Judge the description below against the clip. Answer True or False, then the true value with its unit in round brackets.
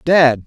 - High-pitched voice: False (140 Hz)